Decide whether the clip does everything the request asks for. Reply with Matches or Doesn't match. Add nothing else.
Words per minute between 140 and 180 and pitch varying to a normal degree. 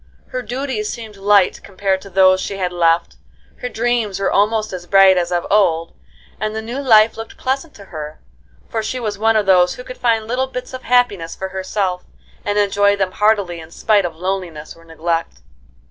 Doesn't match